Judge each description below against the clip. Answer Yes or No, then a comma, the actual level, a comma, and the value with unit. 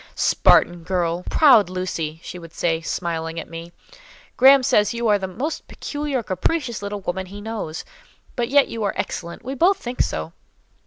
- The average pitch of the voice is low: No, high, 200 Hz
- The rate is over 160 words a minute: Yes, average, 170 wpm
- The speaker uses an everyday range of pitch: No, wide, 6.5 semitones